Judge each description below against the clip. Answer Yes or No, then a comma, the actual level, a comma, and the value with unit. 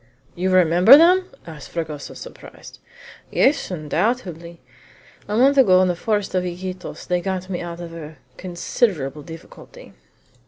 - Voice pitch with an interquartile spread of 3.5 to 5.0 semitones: Yes, average, 3.8 semitones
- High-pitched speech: No, medium, 180 Hz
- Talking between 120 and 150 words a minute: Yes, average, 140 wpm